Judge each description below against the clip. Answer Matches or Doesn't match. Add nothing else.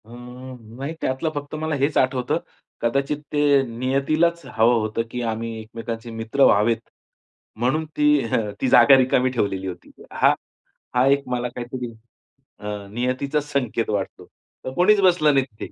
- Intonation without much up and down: Doesn't match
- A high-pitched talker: Doesn't match